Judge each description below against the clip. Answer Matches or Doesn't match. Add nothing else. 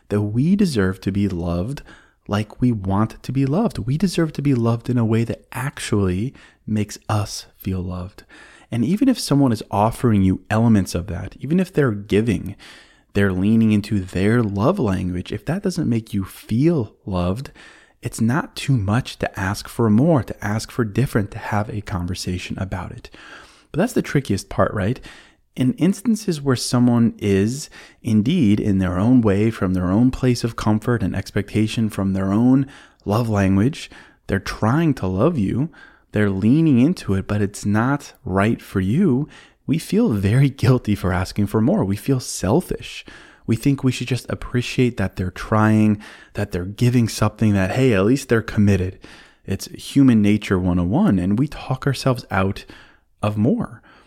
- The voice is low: Matches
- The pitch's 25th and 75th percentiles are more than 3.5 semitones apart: Matches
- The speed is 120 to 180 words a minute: Matches